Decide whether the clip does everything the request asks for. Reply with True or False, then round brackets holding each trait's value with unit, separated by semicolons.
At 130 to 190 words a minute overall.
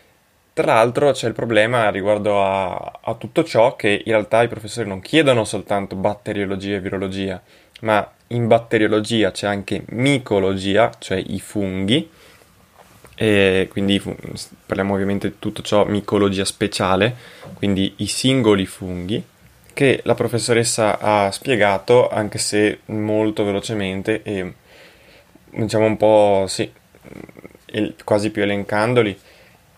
False (120 wpm)